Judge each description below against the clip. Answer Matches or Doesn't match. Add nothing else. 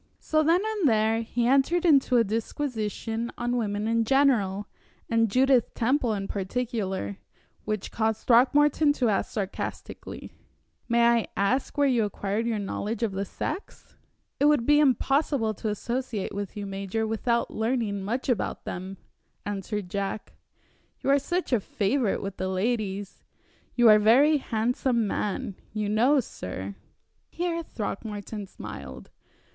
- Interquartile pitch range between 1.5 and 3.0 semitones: Doesn't match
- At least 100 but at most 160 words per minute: Matches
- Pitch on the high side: Matches